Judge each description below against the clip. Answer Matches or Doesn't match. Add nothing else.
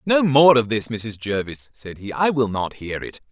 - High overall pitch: Doesn't match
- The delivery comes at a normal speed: Doesn't match